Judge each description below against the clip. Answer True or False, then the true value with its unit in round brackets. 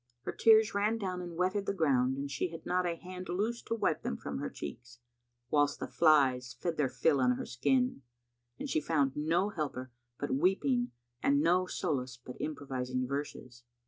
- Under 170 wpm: False (185 wpm)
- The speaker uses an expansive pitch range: True (5.9 semitones)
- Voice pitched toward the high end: False (155 Hz)